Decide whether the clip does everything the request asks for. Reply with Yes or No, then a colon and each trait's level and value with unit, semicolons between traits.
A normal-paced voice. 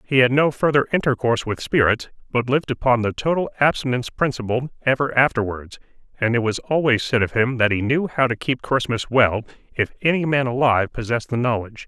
Yes: average, 190 wpm